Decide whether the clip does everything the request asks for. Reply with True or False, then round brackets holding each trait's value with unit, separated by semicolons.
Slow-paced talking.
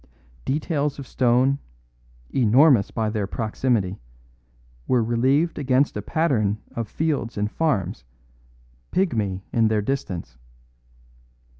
True (105 wpm)